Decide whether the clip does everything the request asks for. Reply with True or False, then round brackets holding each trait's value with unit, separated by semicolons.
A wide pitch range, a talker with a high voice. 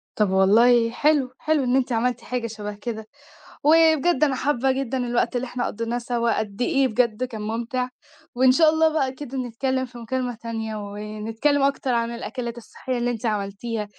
False (2.7 semitones; 245 Hz)